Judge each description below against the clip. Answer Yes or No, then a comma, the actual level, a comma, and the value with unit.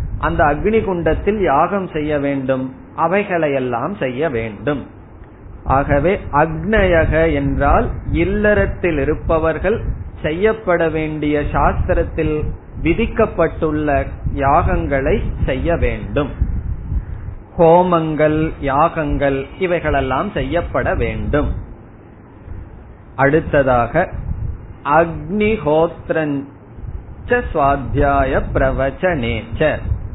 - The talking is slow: Yes, slow, 55 wpm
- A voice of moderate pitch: Yes, medium, 145 Hz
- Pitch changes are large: Yes, wide, 6.0 semitones